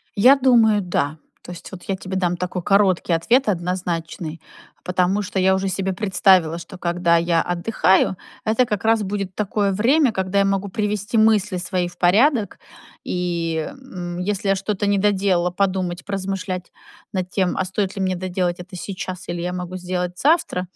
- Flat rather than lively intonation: Yes, narrow, 2.3 semitones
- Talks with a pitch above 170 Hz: Yes, medium, 185 Hz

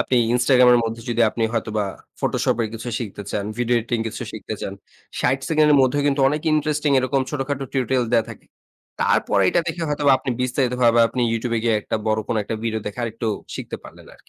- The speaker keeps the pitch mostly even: No, average, 3.4 semitones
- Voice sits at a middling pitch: No, low, 125 Hz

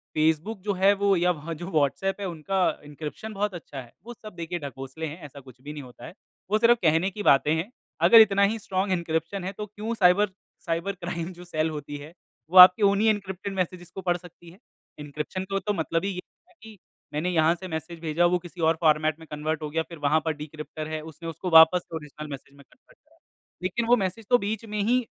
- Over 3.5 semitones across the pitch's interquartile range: Yes, average, 4.0 semitones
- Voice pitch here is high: No, medium, 175 Hz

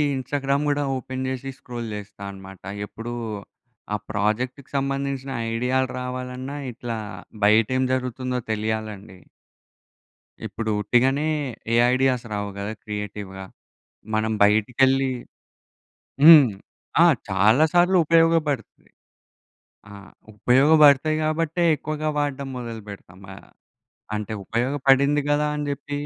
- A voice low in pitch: Yes, low, 130 Hz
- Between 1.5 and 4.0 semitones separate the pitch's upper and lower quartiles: No, average, 4.5 semitones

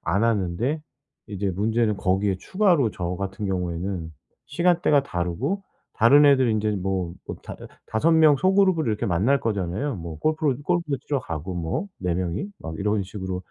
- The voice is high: No, low, 105 Hz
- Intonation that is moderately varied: No, wide, 7.8 semitones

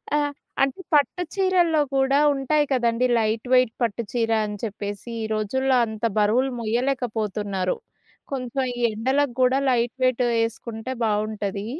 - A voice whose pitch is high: Yes, high, 235 Hz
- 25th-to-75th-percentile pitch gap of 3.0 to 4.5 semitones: Yes, average, 3.7 semitones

